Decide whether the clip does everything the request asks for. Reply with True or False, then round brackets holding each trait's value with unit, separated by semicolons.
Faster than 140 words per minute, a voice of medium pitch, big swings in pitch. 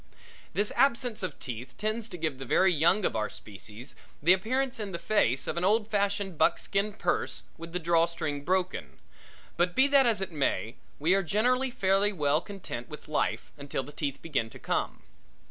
True (190 wpm; 180 Hz; 6.1 semitones)